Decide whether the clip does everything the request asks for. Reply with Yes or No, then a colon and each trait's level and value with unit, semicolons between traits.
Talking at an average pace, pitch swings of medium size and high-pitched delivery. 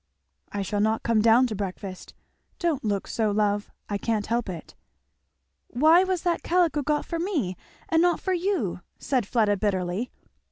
No: average, 165 wpm; wide, 8.2 semitones; high, 230 Hz